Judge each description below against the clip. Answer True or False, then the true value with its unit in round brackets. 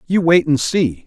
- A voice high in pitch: False (155 Hz)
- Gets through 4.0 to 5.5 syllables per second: True (4.3 syllables/s)